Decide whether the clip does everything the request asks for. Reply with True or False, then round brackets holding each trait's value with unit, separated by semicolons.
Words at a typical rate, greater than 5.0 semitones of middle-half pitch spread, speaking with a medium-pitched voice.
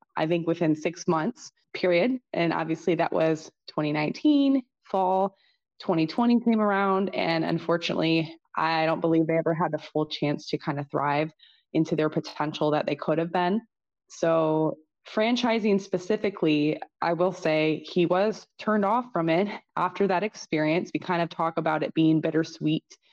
False (160 wpm; 3.6 semitones; 165 Hz)